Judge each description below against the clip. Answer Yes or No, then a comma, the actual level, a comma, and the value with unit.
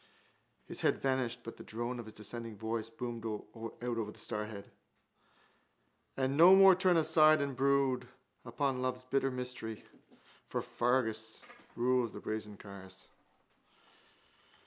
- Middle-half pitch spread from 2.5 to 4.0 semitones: Yes, average, 3.1 semitones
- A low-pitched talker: Yes, low, 120 Hz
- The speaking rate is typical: No, slow, 130 wpm